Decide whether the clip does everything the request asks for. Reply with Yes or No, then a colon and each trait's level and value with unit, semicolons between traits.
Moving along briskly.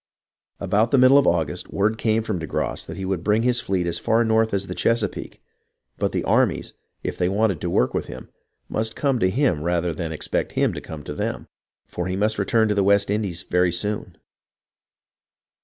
Yes: fast, 210 wpm